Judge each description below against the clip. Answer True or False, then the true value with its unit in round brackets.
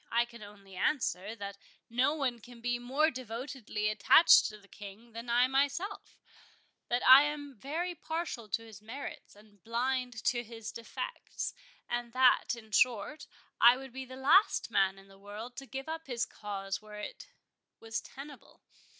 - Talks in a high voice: True (240 Hz)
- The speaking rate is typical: True (160 wpm)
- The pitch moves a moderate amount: True (4.1 semitones)